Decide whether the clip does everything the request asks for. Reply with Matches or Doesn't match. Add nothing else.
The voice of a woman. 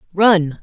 Matches